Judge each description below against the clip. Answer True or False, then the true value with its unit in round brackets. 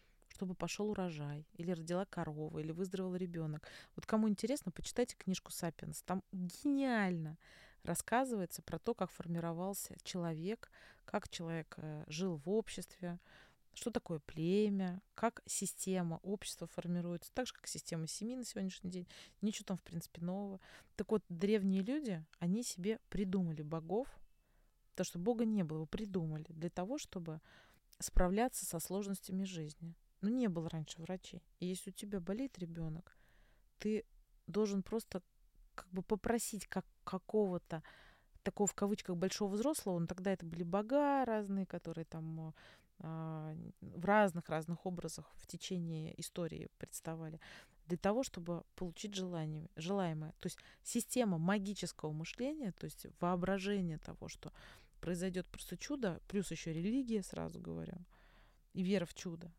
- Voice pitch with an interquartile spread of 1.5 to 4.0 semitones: True (3.5 semitones)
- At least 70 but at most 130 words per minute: False (140 wpm)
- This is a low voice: False (185 Hz)